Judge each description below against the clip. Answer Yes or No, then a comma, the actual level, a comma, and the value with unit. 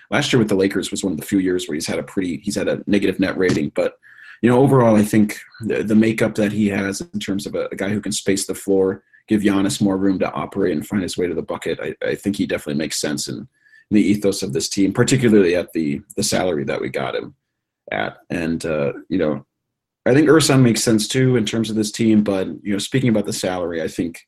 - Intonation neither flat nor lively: Yes, average, 3.4 semitones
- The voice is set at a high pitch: No, low, 105 Hz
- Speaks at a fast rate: Yes, fast, 260 wpm